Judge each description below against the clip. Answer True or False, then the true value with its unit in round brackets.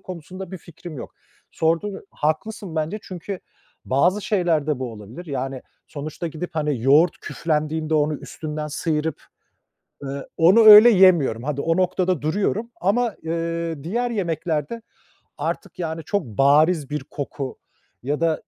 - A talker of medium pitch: True (160 Hz)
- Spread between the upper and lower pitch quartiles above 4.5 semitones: False (3.7 semitones)